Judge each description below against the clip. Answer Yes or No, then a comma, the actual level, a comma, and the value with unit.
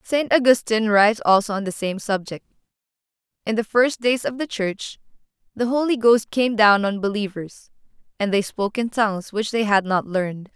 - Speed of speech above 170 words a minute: Yes, average, 180 wpm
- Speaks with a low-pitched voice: No, high, 215 Hz